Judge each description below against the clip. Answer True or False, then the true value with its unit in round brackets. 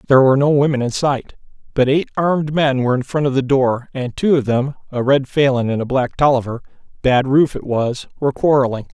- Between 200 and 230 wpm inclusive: True (205 wpm)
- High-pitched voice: False (135 Hz)